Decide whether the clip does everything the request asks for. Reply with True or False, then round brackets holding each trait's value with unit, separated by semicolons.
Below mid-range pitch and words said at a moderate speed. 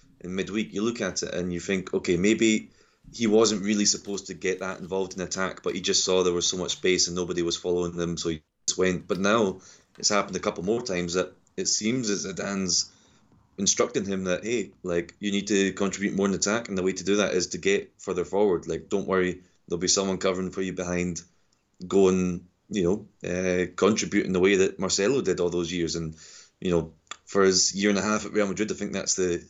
False (95 Hz; 235 wpm)